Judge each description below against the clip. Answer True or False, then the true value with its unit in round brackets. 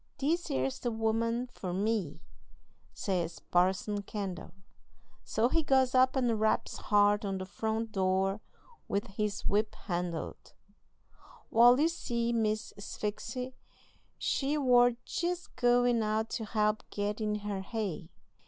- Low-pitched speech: False (215 Hz)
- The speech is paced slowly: True (130 wpm)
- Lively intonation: False (3.5 semitones)